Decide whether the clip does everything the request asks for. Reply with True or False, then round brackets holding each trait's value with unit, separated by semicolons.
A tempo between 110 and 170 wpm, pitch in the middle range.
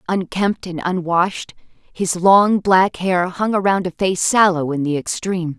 True (160 wpm; 180 Hz)